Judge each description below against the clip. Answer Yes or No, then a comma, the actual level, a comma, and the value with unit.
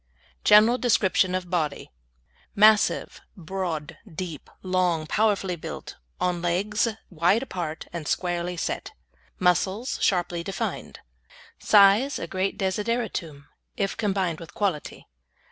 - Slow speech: Yes, slow, 110 wpm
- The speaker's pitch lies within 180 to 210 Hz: Yes, medium, 185 Hz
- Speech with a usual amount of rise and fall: Yes, average, 3.0 semitones